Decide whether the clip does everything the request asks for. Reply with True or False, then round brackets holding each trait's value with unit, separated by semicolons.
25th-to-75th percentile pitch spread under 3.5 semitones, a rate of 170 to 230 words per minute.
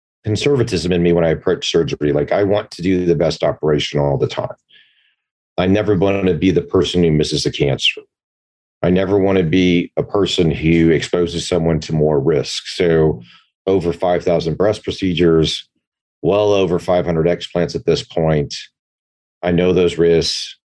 True (2.9 semitones; 175 wpm)